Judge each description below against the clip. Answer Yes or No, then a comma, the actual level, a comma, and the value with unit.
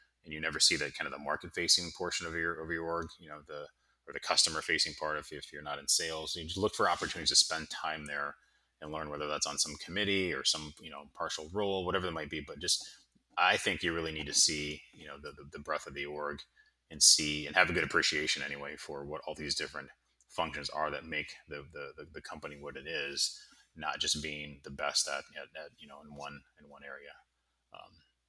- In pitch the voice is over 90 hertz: No, very low, 75 Hz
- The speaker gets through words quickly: Yes, fast, 240 wpm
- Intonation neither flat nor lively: No, narrow, 2.1 semitones